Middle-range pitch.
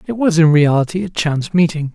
Yes: medium, 165 Hz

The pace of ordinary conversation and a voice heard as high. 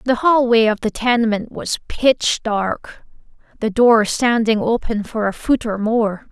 Yes: average, 160 wpm; high, 225 Hz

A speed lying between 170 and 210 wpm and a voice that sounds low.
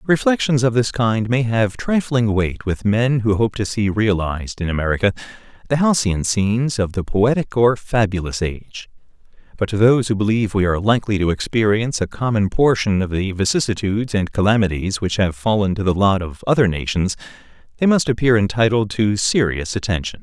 Yes: average, 180 wpm; low, 105 Hz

